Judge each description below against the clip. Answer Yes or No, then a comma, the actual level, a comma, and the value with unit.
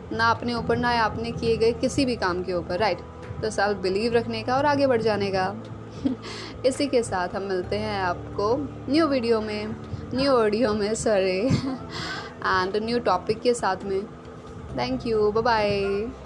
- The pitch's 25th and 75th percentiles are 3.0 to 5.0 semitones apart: Yes, average, 3.4 semitones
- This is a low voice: No, high, 220 Hz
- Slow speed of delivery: No, average, 180 wpm